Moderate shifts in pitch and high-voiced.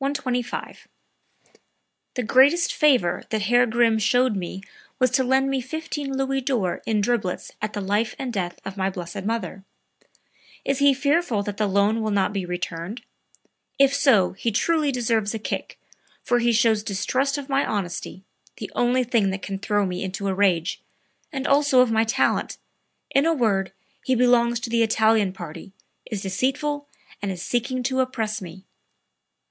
Yes: average, 4.8 semitones; high, 225 Hz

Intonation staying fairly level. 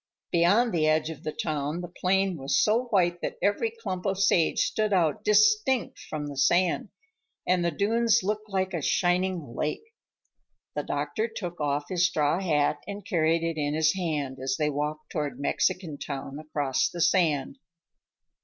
No: average, 4.5 semitones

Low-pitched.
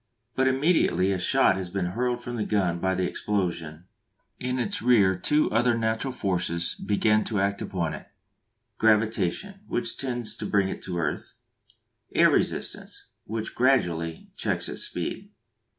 Yes: low, 105 Hz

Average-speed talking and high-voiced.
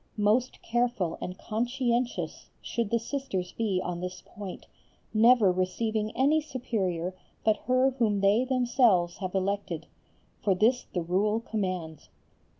No: slow, 130 wpm; high, 215 Hz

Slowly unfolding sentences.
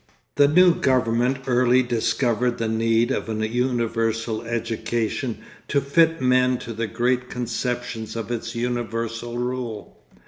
Yes: slow, 130 wpm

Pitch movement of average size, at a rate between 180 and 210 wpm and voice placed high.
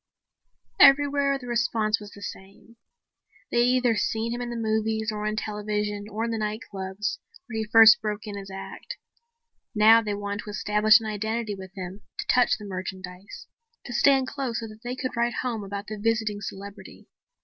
No: narrow, 2.2 semitones; average, 185 wpm; high, 215 Hz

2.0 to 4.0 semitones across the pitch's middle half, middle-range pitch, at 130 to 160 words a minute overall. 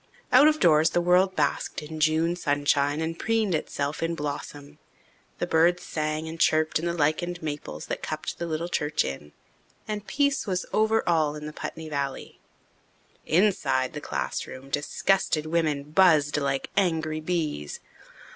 Yes: average, 3.0 semitones; medium, 160 Hz; average, 150 wpm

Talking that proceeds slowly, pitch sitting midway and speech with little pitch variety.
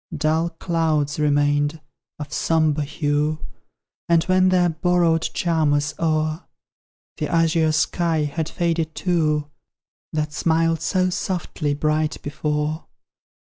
Yes: slow, 110 wpm; medium, 155 Hz; narrow, 1.8 semitones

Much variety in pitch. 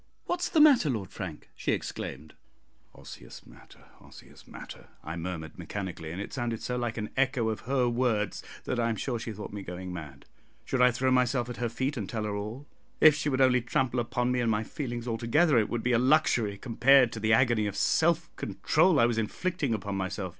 No: average, 3.8 semitones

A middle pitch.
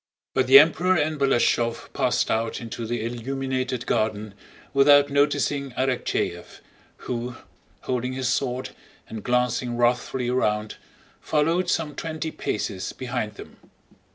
No: low, 130 Hz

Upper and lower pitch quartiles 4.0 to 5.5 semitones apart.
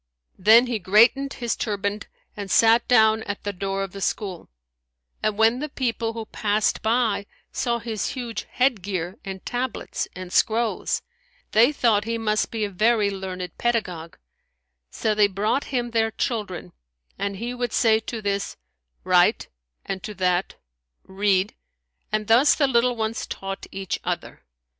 No: average, 3.0 semitones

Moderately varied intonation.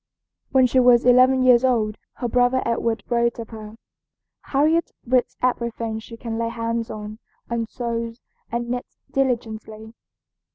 No: narrow, 1.7 semitones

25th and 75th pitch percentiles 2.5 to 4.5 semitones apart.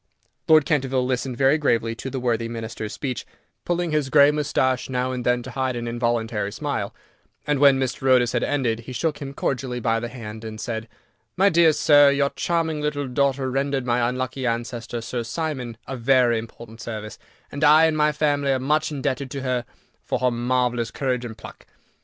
Yes: average, 3.1 semitones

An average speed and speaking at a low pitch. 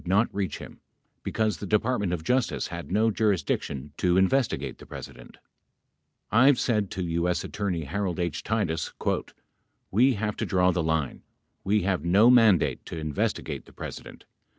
Yes: average, 160 wpm; very low, 95 Hz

